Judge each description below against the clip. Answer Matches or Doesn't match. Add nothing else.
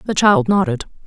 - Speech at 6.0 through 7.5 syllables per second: Doesn't match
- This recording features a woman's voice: Matches